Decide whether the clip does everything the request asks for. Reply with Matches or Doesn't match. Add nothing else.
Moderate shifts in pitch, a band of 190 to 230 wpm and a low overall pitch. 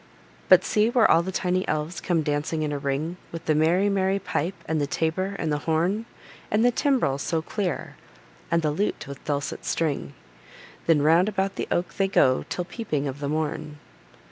Doesn't match